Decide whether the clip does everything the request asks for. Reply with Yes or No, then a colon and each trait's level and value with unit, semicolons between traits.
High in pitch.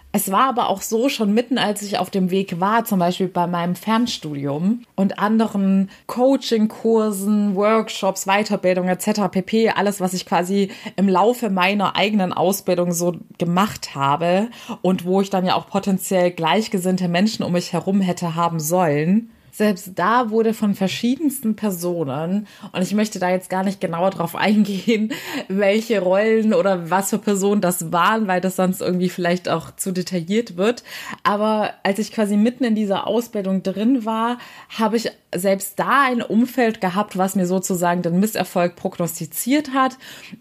Yes: high, 195 Hz